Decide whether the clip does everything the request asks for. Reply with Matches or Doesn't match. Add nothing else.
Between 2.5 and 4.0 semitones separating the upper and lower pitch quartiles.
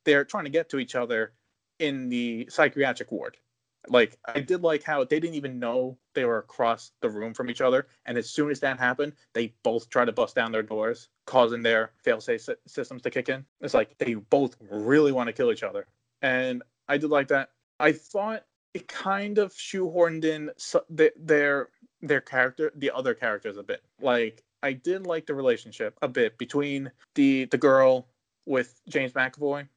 Doesn't match